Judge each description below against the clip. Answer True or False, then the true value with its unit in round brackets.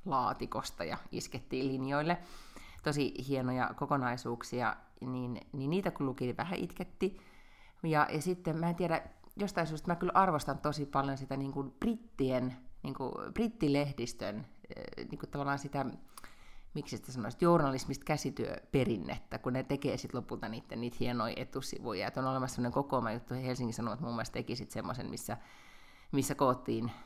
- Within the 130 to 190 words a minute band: True (150 wpm)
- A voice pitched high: False (140 Hz)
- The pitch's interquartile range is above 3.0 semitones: True (3.8 semitones)